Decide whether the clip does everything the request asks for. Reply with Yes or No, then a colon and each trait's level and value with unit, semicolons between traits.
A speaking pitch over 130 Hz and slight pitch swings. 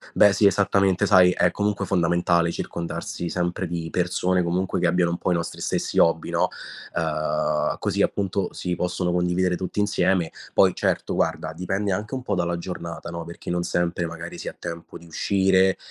No: very low, 90 Hz; narrow, 1.9 semitones